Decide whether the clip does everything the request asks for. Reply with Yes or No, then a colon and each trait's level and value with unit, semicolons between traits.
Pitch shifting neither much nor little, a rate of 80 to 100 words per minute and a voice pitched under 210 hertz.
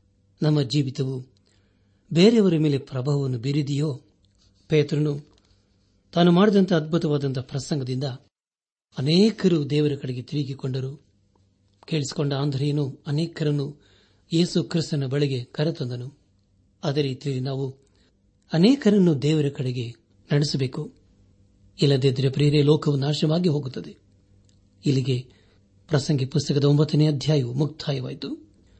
No: wide, 6.8 semitones; average, 85 wpm; medium, 140 Hz